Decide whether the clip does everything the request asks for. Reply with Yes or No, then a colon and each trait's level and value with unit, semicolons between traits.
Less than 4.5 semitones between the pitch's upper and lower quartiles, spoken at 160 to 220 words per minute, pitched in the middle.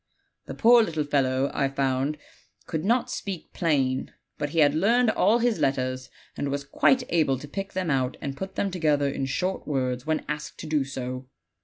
No: average, 5.2 semitones; average, 190 wpm; medium, 145 Hz